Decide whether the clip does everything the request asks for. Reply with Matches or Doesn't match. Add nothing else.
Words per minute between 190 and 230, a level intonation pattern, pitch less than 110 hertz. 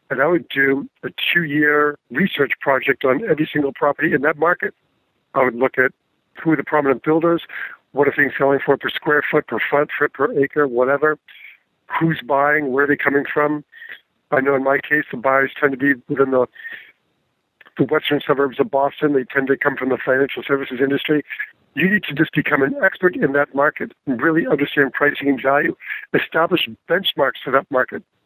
Doesn't match